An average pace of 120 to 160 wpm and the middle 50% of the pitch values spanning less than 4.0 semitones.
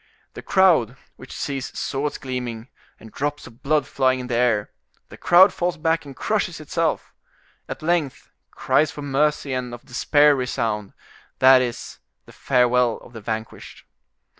Yes: average, 150 wpm; average, 3.4 semitones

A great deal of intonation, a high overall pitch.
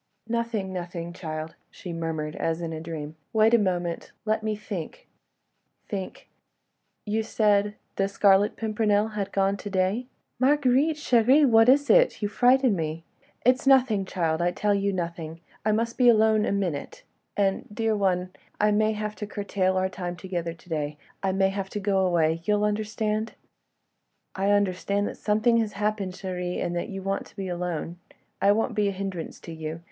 No: average, 3.5 semitones; high, 200 Hz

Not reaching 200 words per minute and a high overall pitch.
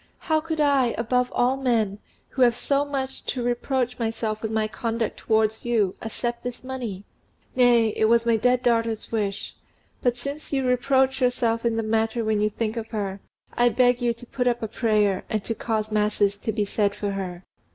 No: fast, 205 wpm; high, 230 Hz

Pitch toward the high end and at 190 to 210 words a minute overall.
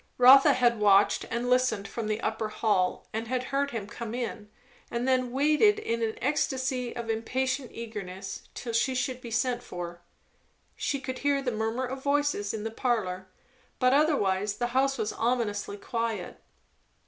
No: high, 235 Hz; average, 165 wpm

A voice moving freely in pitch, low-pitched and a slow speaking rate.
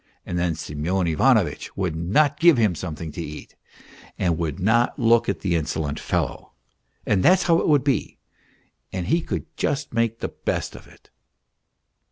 No: wide, 7.3 semitones; very low, 95 Hz; average, 175 wpm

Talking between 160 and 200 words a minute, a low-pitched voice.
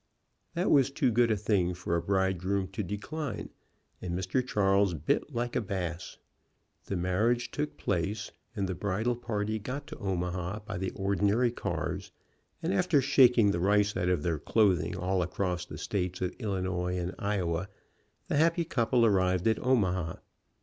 Yes: average, 165 wpm; low, 100 Hz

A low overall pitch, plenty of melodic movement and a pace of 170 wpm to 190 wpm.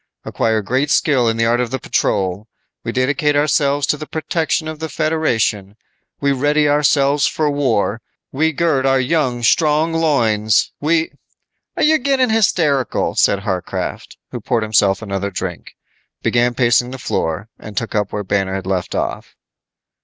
No: low, 130 Hz; wide, 5.9 semitones; average, 160 wpm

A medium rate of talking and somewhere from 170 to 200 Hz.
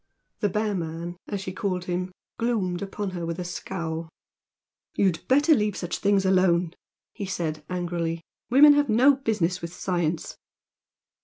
Yes: average, 150 wpm; medium, 185 Hz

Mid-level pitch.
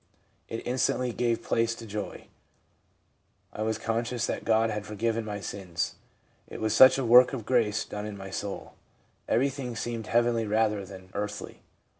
No: low, 110 Hz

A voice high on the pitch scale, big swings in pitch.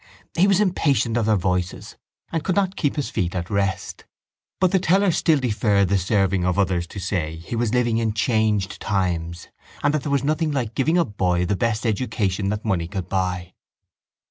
No: low, 105 Hz; wide, 7.0 semitones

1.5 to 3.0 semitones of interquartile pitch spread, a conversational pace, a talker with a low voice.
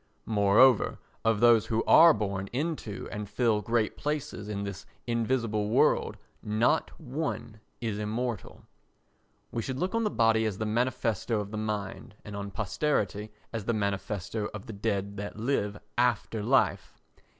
Yes: average, 2.7 semitones; average, 150 wpm; low, 110 Hz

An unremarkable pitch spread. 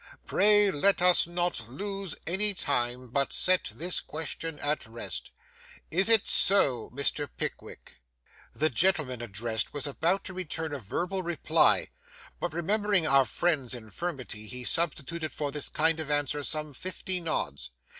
No: wide, 5.8 semitones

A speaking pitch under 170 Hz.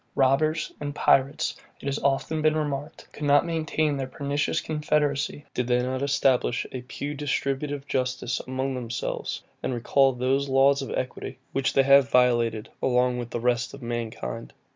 Yes: low, 135 Hz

